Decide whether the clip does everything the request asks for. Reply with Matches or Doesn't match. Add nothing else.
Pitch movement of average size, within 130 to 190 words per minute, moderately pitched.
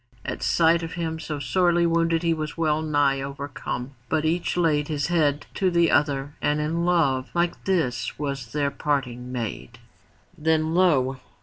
Matches